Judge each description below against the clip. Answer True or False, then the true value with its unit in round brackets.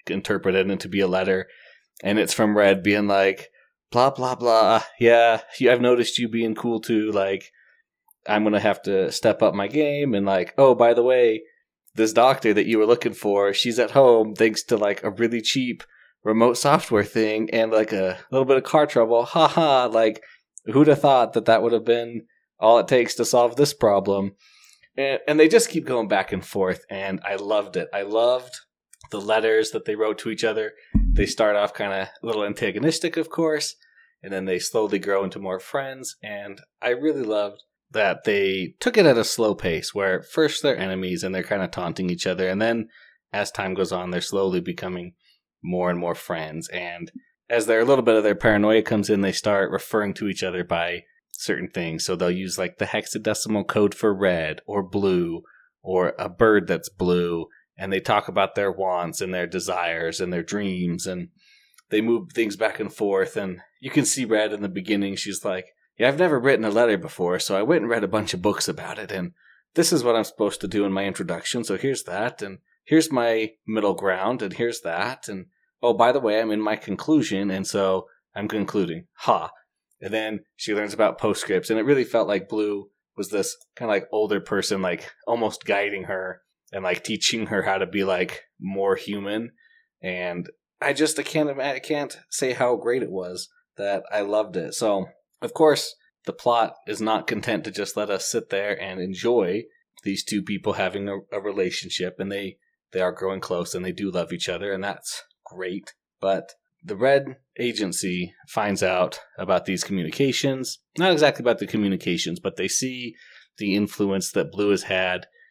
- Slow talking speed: False (200 wpm)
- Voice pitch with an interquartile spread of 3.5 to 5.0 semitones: True (3.9 semitones)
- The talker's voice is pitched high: False (105 Hz)